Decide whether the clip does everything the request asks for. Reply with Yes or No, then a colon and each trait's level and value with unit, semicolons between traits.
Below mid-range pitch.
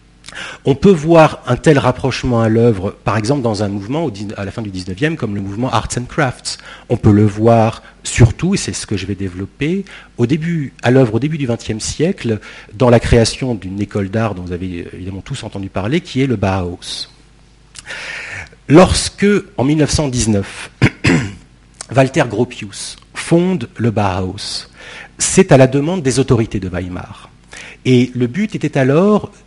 Yes: low, 120 Hz